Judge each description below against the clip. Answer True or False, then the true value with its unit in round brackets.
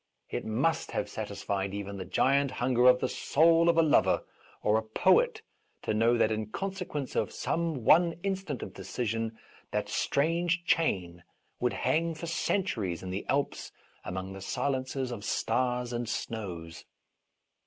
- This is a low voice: True (125 Hz)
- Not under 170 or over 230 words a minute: False (155 wpm)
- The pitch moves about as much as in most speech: False (7.3 semitones)